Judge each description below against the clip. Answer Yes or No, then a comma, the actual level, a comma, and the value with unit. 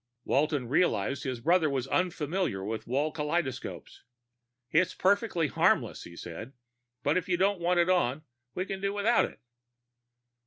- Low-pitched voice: No, medium, 160 Hz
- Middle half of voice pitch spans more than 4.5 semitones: Yes, wide, 5.6 semitones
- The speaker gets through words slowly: No, average, 150 wpm